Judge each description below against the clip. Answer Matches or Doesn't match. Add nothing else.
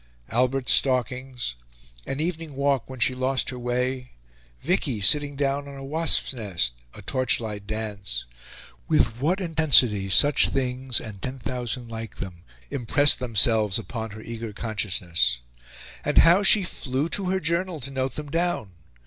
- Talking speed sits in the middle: Matches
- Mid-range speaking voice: Doesn't match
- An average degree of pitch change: Matches